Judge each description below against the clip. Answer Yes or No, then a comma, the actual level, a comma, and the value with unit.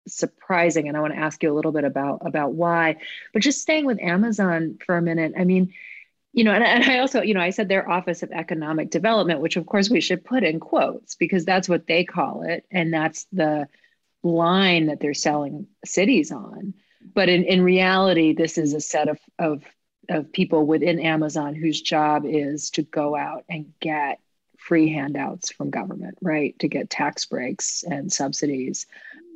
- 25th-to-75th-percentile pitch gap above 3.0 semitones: Yes, average, 3.5 semitones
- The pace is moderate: Yes, average, 190 wpm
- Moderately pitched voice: Yes, medium, 170 Hz